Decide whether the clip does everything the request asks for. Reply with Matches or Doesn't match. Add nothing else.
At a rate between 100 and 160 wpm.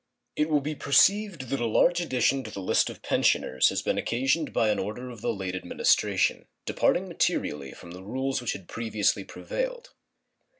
Doesn't match